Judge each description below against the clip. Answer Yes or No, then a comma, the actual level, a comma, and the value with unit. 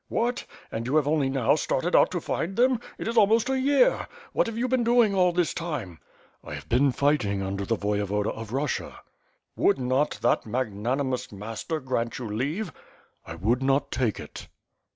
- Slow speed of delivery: No, average, 185 wpm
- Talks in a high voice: No, low, 135 Hz